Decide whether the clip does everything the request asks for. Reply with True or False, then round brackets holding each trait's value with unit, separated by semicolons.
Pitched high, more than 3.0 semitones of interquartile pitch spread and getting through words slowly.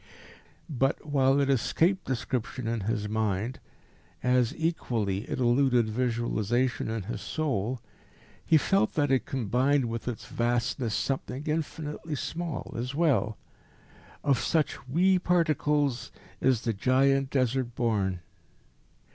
False (130 Hz; 3.7 semitones; 120 wpm)